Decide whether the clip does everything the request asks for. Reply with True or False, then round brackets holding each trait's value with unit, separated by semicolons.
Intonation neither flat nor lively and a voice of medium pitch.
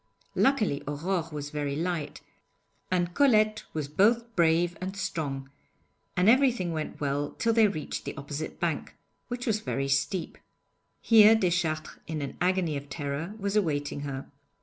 False (6.3 semitones; 170 Hz)